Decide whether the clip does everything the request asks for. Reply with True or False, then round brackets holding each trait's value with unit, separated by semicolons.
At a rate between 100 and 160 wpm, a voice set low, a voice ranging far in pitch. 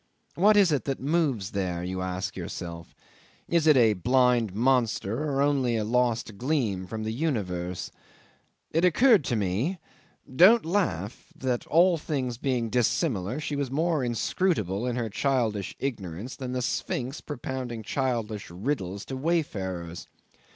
True (145 wpm; 125 Hz; 6.2 semitones)